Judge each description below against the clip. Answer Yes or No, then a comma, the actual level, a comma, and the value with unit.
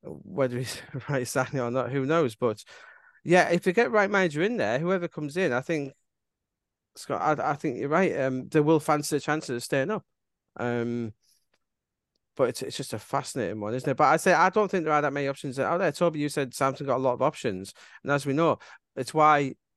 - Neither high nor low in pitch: Yes, medium, 145 Hz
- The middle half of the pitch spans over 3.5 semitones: Yes, average, 4.5 semitones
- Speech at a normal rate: No, fast, 230 wpm